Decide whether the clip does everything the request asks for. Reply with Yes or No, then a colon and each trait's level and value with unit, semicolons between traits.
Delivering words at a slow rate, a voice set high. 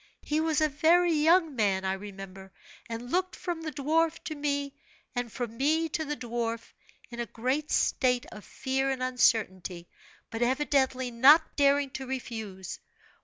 No: average, 160 wpm; very high, 265 Hz